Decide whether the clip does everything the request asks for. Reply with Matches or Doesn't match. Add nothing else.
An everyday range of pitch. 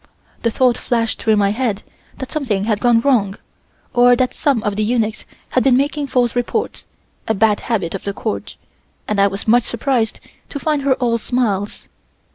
Matches